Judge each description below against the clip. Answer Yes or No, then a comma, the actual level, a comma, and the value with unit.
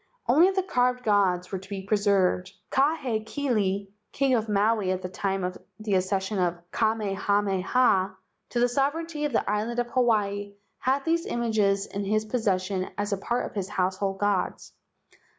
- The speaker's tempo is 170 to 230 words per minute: No, average, 160 wpm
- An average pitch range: Yes, average, 4.0 semitones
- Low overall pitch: No, high, 205 Hz